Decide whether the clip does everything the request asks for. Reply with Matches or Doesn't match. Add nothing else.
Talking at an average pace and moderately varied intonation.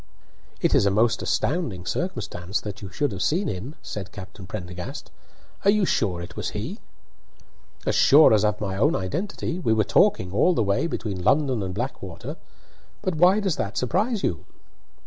Doesn't match